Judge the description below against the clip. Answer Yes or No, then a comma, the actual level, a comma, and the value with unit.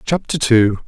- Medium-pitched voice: No, low, 125 Hz